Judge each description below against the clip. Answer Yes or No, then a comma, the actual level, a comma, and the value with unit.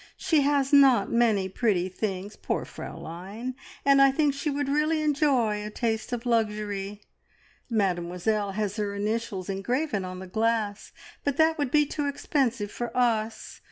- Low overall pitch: No, high, 225 Hz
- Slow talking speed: No, average, 155 wpm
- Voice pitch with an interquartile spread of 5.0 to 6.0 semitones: Yes, average, 5.3 semitones